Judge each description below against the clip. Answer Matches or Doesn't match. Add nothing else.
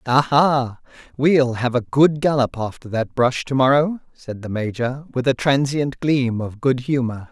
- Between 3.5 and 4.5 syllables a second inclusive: Matches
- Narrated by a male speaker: Matches